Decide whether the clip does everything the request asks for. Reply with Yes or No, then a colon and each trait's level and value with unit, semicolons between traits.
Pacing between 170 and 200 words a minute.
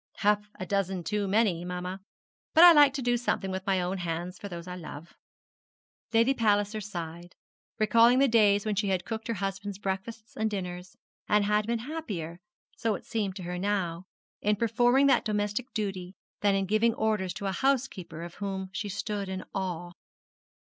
Yes: average, 180 wpm